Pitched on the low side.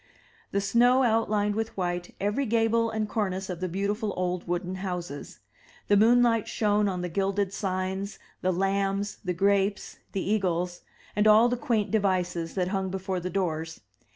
No: high, 195 Hz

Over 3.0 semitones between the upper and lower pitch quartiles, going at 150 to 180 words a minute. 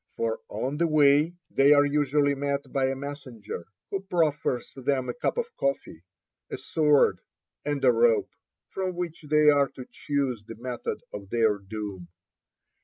Yes: average, 3.7 semitones; average, 160 wpm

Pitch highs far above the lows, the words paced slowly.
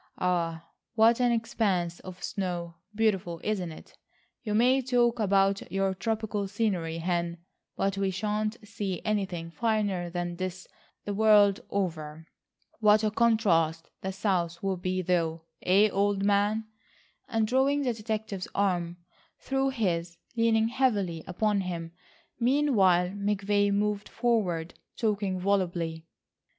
No: average, 3.7 semitones; slow, 125 wpm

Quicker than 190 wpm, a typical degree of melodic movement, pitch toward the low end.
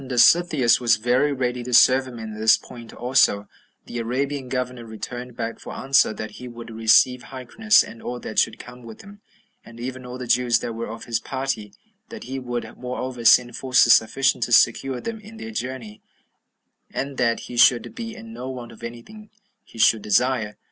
No: average, 200 wpm; narrow, 2.3 semitones; low, 125 Hz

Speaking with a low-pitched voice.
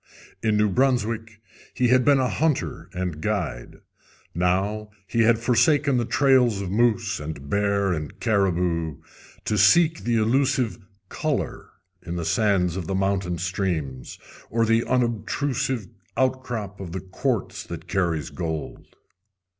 Yes: low, 105 Hz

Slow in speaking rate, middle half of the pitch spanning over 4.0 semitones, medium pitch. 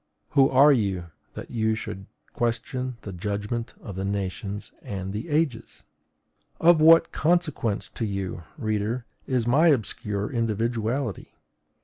No: slow, 125 wpm; average, 4.4 semitones; low, 115 Hz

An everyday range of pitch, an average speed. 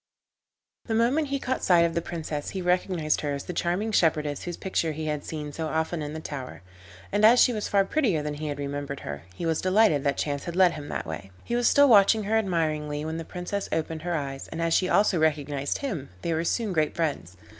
No: average, 4.6 semitones; fast, 235 wpm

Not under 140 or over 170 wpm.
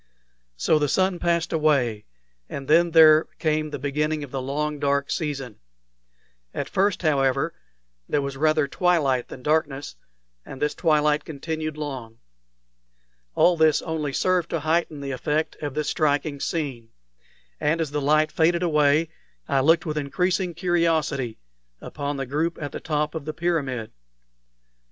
Yes: average, 150 wpm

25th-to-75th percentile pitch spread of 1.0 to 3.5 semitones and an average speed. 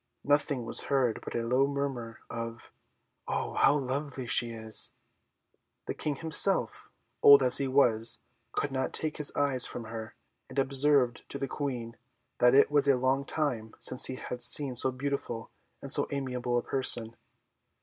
Yes: average, 2.8 semitones; average, 165 wpm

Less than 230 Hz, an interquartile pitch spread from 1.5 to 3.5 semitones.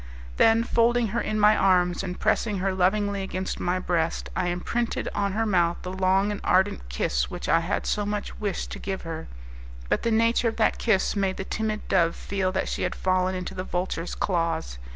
Yes: high, 190 Hz; average, 2.8 semitones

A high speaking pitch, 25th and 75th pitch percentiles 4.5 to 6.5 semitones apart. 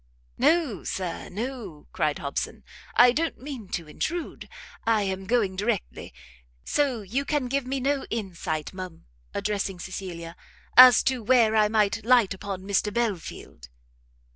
Yes: high, 210 Hz; average, 5.1 semitones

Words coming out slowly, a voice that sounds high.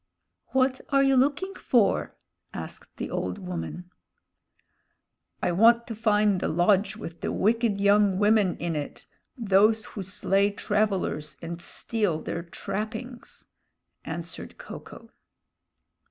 Yes: slow, 125 wpm; high, 205 Hz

